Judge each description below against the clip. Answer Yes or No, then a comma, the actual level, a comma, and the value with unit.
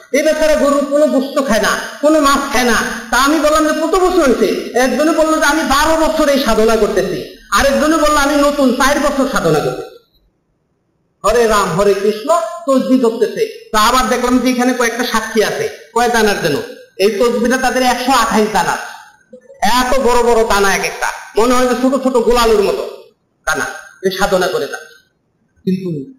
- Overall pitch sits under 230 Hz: No, very high, 265 Hz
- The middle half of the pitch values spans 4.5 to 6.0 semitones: Yes, average, 5.3 semitones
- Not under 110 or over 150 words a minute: No, fast, 175 wpm